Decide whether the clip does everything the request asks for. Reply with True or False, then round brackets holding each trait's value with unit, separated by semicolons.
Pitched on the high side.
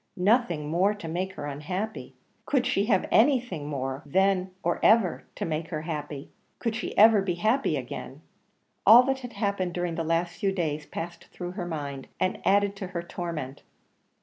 False (180 Hz)